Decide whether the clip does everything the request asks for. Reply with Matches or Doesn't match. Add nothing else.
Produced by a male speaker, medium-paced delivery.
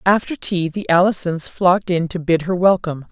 Doesn't match